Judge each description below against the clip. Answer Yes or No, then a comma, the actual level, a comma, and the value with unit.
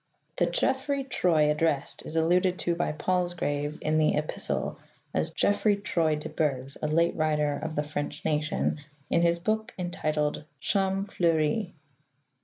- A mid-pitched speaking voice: Yes, medium, 160 Hz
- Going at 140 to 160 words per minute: Yes, average, 155 wpm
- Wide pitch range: No, average, 3.2 semitones